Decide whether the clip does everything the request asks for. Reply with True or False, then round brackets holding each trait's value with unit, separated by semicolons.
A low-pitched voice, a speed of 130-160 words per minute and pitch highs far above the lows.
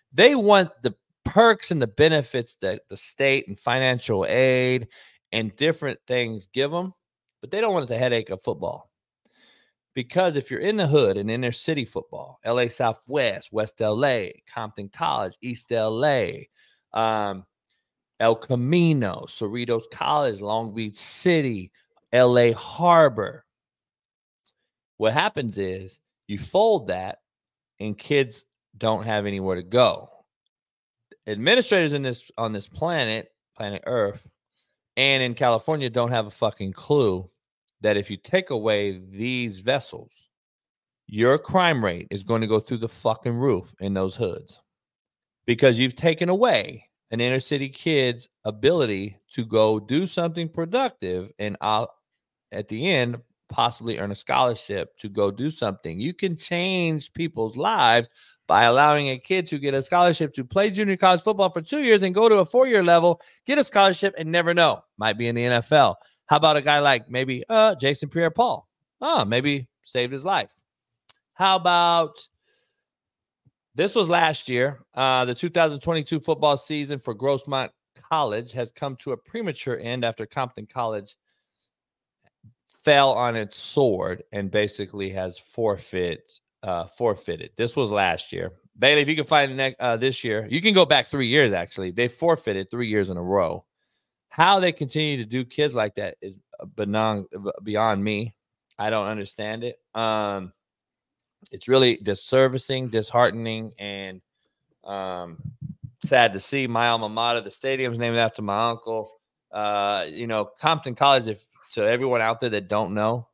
True (125 Hz; 155 wpm; 5.7 semitones)